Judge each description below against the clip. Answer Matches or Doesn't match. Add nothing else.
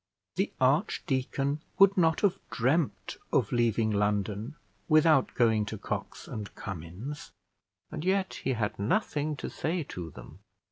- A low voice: Matches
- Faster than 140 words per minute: Doesn't match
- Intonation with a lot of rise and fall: Matches